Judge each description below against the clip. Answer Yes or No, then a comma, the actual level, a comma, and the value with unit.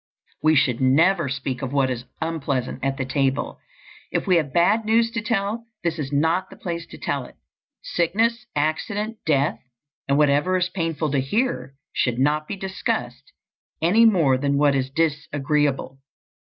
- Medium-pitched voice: Yes, medium, 150 Hz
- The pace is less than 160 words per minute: No, average, 165 wpm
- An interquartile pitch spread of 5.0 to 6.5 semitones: Yes, average, 5.3 semitones